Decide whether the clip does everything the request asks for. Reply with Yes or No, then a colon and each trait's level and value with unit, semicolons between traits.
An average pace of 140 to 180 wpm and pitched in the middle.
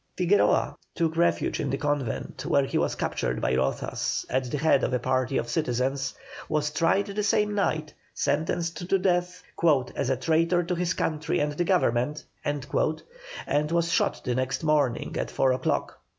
Yes: average, 170 wpm; medium, 150 Hz